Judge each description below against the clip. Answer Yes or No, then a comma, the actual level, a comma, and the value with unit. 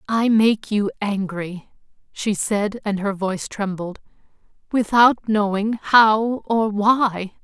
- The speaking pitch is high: Yes, high, 210 Hz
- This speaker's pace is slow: Yes, slow, 120 wpm